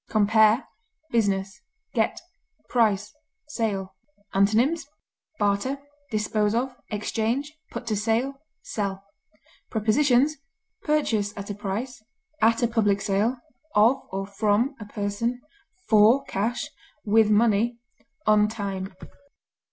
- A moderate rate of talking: No, slow, 105 wpm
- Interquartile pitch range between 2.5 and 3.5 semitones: Yes, average, 2.8 semitones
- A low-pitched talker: No, high, 215 Hz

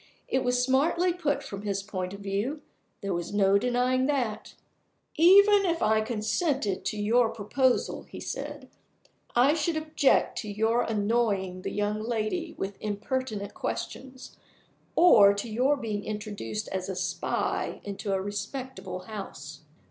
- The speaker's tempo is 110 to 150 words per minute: Yes, average, 140 wpm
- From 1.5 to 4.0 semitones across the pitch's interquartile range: No, average, 4.7 semitones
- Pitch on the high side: Yes, high, 220 Hz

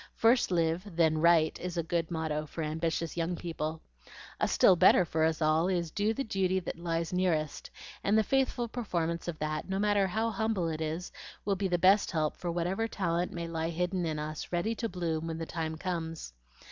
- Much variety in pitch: No, average, 2.8 semitones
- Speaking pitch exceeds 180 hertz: No, medium, 170 Hz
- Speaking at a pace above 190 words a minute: Yes, fast, 205 wpm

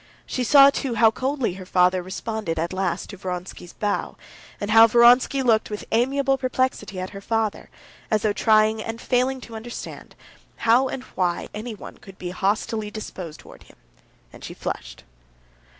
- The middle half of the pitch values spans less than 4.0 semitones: No, average, 4.3 semitones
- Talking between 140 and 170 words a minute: Yes, average, 165 wpm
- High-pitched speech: Yes, high, 220 Hz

